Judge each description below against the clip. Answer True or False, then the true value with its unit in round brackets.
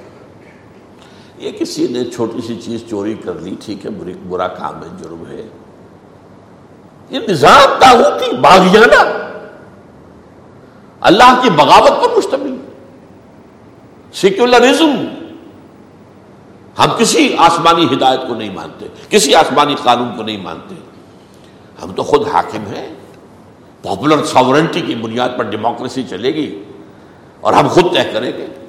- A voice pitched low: True (130 Hz)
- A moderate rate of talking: True (125 wpm)